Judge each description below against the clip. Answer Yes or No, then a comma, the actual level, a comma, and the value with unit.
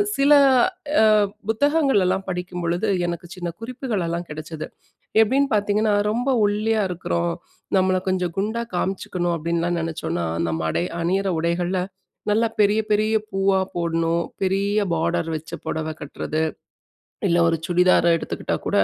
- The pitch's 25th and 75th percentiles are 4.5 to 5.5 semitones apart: No, average, 3.6 semitones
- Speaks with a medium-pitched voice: Yes, medium, 180 Hz